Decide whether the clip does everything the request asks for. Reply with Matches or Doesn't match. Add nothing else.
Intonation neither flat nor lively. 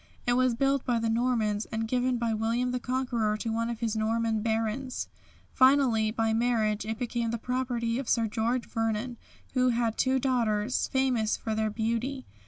Doesn't match